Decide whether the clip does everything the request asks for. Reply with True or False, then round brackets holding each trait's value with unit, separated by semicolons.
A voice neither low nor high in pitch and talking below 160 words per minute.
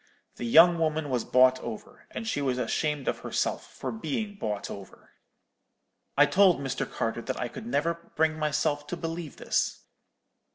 False (150 Hz; 165 wpm)